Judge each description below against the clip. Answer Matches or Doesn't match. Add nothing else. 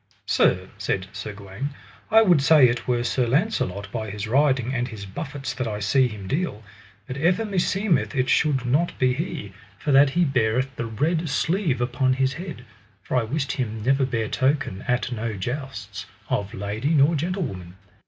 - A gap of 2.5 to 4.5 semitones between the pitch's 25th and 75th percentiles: Doesn't match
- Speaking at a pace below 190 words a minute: Matches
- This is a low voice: Matches